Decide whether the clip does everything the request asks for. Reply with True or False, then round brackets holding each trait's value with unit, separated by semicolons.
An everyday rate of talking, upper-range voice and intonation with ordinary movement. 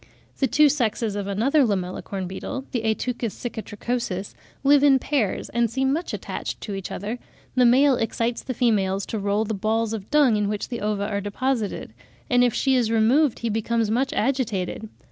True (185 wpm; 225 Hz; 3.8 semitones)